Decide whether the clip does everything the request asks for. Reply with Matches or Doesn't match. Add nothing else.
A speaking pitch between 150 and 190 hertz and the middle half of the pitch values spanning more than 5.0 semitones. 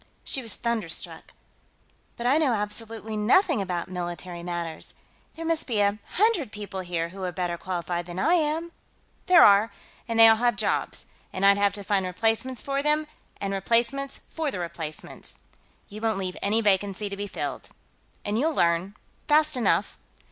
Doesn't match